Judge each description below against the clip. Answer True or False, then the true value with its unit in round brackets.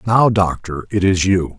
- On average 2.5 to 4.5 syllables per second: True (4.3 syllables/s)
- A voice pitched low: True (95 Hz)